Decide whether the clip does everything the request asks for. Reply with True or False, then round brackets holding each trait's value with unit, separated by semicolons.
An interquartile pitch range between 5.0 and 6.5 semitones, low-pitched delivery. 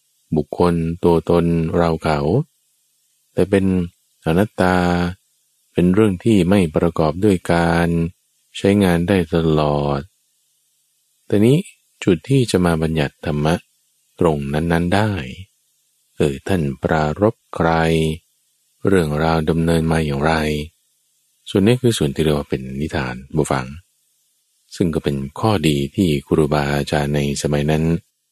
False (3.5 semitones; 85 Hz)